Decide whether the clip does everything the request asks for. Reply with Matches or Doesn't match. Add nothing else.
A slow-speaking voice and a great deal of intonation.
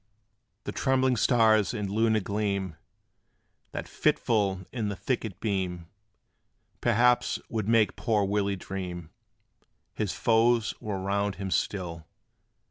Doesn't match